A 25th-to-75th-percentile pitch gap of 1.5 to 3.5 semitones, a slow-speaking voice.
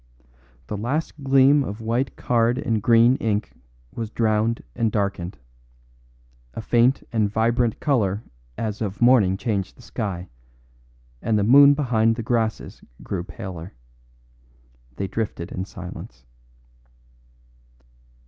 Yes: average, 3.1 semitones; slow, 120 wpm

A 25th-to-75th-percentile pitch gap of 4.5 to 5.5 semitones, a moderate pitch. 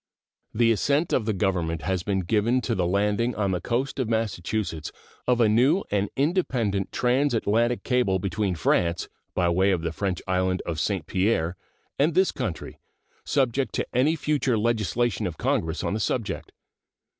No: average, 4.9 semitones; low, 105 Hz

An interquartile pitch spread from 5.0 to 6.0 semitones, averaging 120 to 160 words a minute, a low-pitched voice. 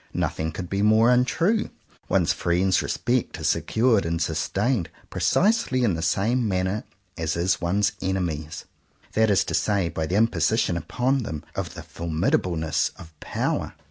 Yes: wide, 5.4 semitones; average, 155 wpm; very low, 95 Hz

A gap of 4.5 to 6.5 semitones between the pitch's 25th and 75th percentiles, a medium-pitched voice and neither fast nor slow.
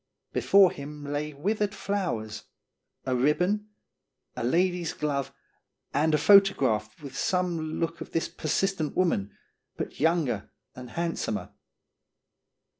No: average, 4.8 semitones; medium, 155 Hz; slow, 115 wpm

